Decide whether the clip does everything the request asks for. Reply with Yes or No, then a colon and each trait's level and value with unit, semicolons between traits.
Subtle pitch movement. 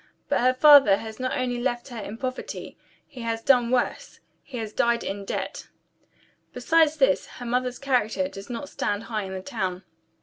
No: average, 3.0 semitones